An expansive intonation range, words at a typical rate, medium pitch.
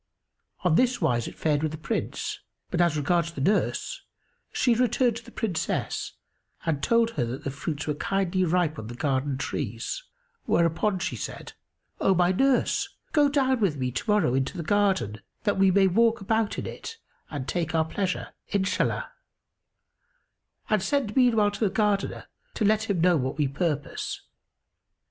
Yes: wide, 6.2 semitones; average, 165 wpm; medium, 180 Hz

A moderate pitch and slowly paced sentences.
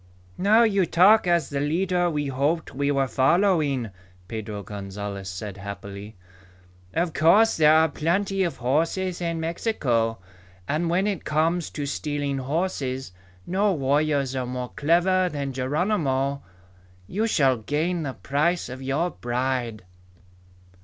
Yes: medium, 145 Hz; slow, 130 wpm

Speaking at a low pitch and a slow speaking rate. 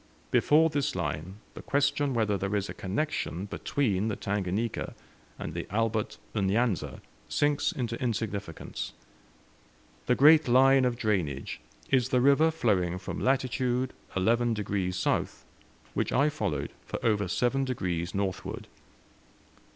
Yes: low, 115 Hz; slow, 130 wpm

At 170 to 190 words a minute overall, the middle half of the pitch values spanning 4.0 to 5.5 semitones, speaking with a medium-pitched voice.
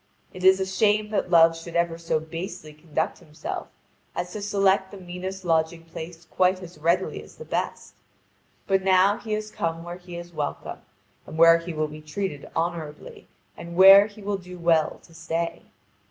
No: average, 185 wpm; narrow, 2.6 semitones; medium, 175 Hz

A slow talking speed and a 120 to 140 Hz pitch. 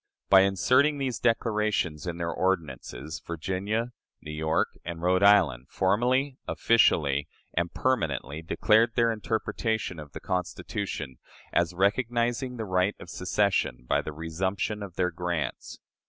No: slow, 130 wpm; very low, 95 Hz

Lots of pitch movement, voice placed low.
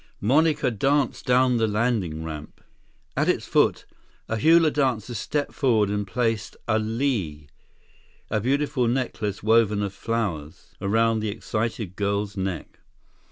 No: average, 3.7 semitones; low, 110 Hz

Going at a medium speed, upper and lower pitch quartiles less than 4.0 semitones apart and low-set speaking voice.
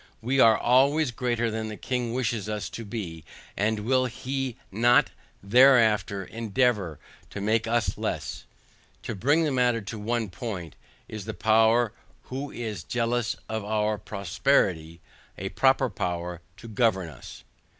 Yes: average, 145 wpm; average, 3.4 semitones; low, 110 Hz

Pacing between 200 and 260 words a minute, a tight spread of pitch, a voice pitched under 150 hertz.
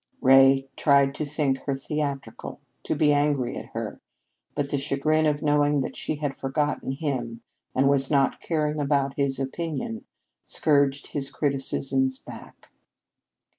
No: average, 140 wpm; narrow, 1.6 semitones; medium, 140 Hz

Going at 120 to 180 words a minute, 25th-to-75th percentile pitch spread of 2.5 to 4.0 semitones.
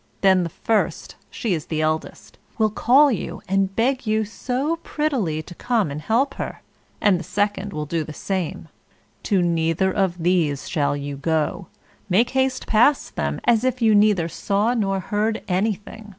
No: average, 170 wpm; average, 5.2 semitones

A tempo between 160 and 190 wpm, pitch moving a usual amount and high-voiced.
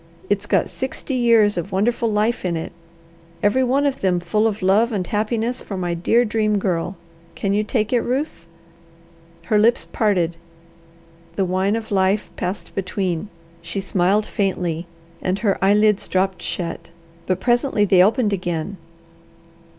No: average, 150 wpm; average, 3.2 semitones; high, 205 Hz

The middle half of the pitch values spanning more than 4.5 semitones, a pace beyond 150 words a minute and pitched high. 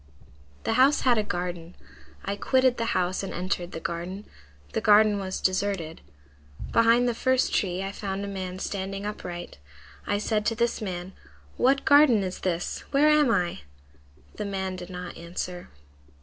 No: average, 4.1 semitones; average, 165 wpm; high, 195 Hz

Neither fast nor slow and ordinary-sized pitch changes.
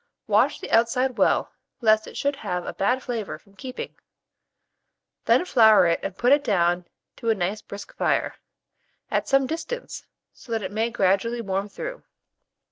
Yes: average, 165 wpm; average, 4.6 semitones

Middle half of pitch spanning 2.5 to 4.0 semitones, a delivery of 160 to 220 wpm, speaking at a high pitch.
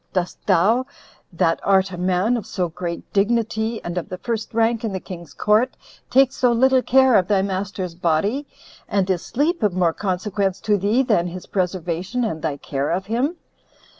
No: average, 4.4 semitones; average, 185 wpm; high, 195 Hz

